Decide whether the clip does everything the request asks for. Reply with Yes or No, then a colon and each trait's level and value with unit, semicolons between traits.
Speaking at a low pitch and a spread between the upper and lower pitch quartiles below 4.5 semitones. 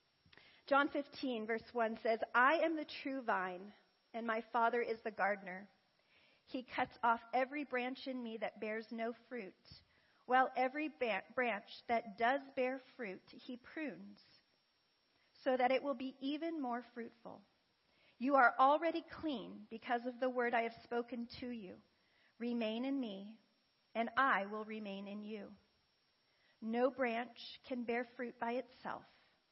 No: high, 240 Hz; narrow, 2.6 semitones